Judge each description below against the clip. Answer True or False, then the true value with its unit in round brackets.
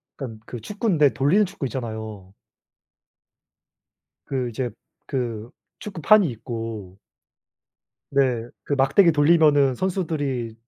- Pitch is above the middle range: False (135 Hz)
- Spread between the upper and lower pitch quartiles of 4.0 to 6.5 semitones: True (5.5 semitones)